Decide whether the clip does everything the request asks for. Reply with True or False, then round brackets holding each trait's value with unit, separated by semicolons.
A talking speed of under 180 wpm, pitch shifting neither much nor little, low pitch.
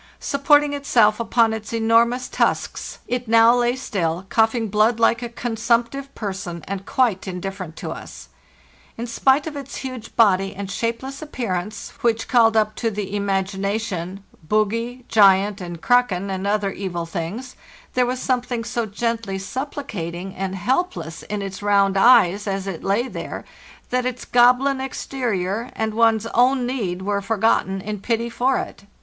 False (155 wpm; 4.0 semitones; 220 Hz)